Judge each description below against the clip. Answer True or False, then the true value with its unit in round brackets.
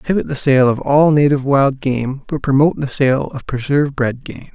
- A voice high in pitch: False (135 Hz)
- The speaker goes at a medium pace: False (210 wpm)